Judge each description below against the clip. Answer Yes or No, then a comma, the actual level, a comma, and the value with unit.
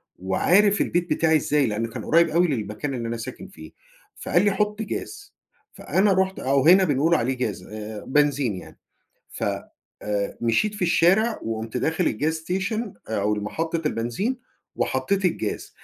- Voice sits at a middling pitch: Yes, medium, 155 Hz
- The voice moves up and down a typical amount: No, wide, 8.8 semitones